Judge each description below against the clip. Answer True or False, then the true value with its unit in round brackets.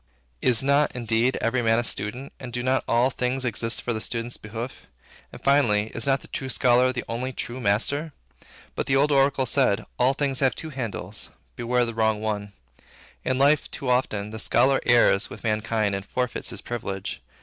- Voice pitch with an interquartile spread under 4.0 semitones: True (2.9 semitones)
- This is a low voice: True (120 Hz)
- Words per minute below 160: False (195 wpm)